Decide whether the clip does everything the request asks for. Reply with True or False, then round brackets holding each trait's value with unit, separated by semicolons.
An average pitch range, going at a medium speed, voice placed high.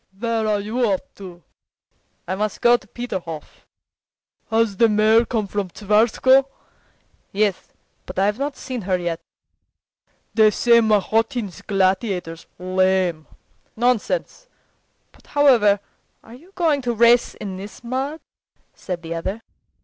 False (4.0 semitones; 125 wpm; 215 Hz)